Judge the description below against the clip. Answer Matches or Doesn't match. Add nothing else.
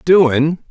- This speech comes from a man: Matches